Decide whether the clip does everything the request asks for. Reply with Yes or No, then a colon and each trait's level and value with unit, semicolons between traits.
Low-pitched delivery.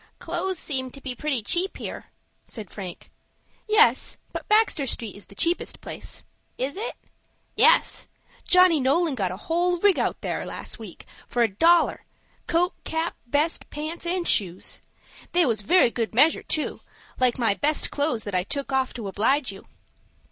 No: very high, 285 Hz